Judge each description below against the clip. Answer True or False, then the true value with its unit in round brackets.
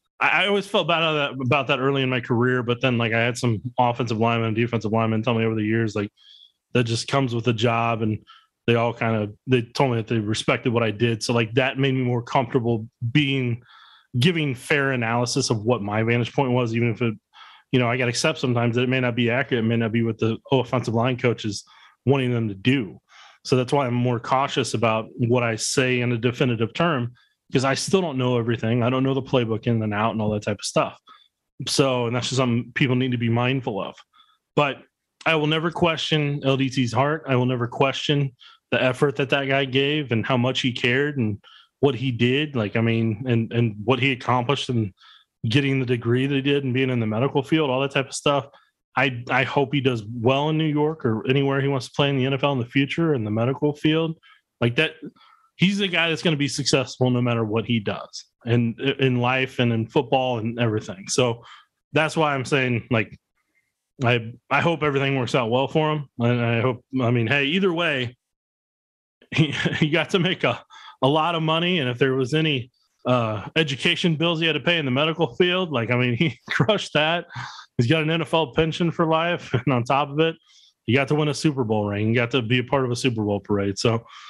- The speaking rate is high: True (230 wpm)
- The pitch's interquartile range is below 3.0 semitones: False (3.4 semitones)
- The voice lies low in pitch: True (130 Hz)